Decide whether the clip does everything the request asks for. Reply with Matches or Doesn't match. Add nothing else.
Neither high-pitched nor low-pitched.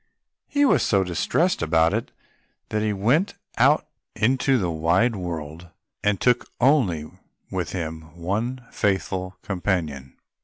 Doesn't match